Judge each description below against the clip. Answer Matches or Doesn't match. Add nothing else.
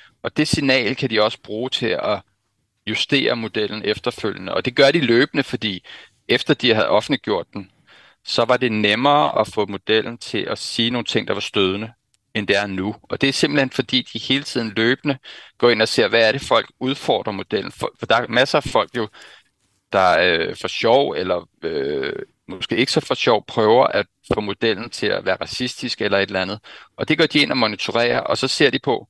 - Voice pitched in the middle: Doesn't match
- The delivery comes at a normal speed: Matches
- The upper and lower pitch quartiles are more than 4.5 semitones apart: Doesn't match